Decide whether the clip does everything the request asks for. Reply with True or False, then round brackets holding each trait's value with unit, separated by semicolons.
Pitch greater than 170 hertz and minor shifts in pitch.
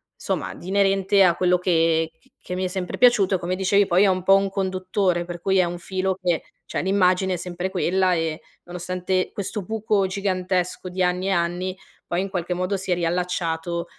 True (185 Hz; 1.6 semitones)